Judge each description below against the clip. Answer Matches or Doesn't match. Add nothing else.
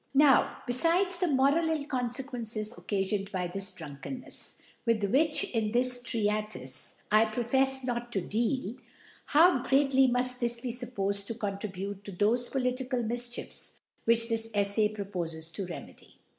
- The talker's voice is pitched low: Doesn't match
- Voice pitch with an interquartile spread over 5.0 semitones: Doesn't match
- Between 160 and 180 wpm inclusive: Doesn't match